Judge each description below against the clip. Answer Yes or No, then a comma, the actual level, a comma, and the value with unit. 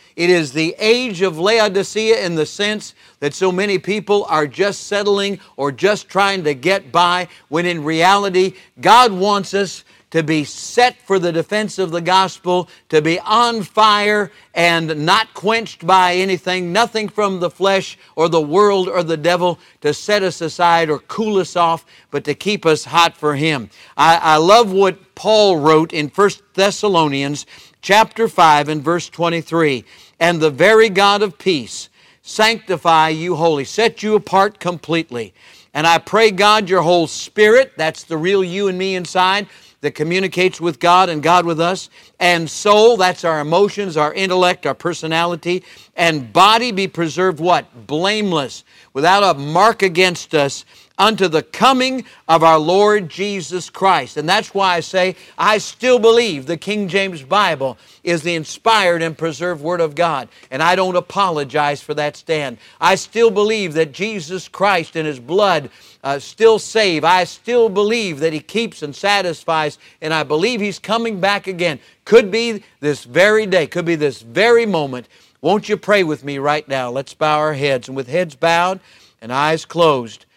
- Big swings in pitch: No, average, 4.2 semitones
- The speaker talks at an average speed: Yes, average, 170 wpm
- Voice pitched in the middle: Yes, medium, 180 Hz